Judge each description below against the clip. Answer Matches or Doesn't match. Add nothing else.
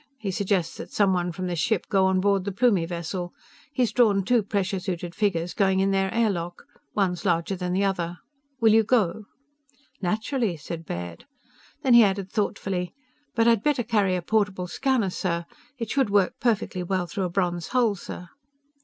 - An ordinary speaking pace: Matches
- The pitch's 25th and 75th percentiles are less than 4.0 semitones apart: Matches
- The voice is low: Doesn't match